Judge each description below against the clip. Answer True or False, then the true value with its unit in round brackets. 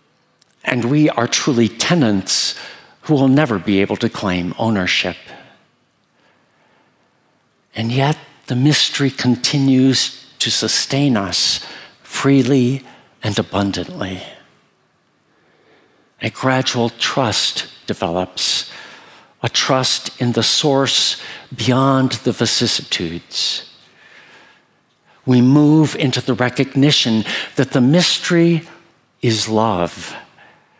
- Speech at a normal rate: False (90 wpm)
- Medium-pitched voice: False (125 Hz)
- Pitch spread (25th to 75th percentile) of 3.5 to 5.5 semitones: True (3.9 semitones)